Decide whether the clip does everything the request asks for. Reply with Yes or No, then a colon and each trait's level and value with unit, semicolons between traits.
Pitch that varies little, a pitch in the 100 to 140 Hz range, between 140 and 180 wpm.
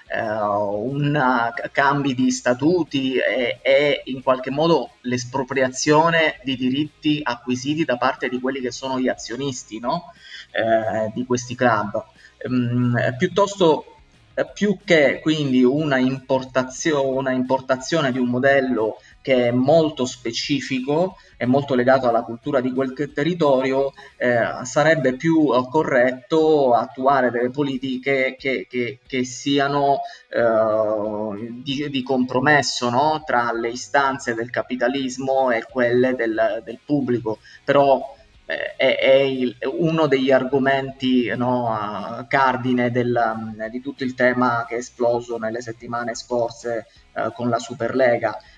No: narrow, 2.3 semitones; low, 130 Hz; average, 130 wpm